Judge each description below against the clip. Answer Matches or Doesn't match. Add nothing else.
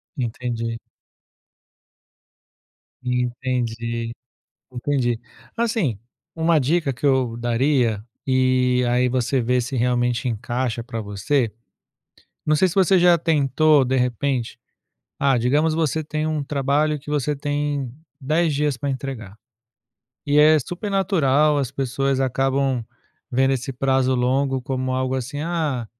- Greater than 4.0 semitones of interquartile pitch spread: Doesn't match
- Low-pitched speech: Matches